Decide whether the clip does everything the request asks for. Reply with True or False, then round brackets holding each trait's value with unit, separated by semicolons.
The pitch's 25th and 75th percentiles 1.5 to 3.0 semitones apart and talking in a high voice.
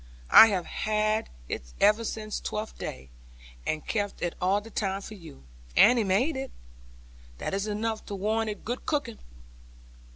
True (2.5 semitones; 210 Hz)